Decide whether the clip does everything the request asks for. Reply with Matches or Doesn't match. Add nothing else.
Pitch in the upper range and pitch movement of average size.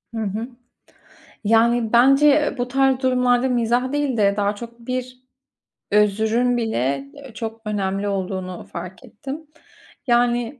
Matches